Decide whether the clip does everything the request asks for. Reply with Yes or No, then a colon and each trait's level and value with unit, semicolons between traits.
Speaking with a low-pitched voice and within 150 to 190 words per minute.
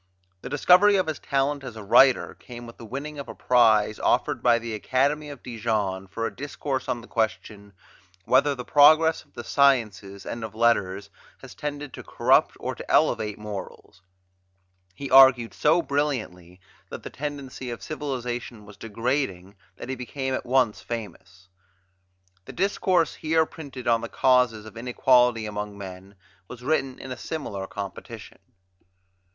Yes: low, 120 Hz; average, 160 wpm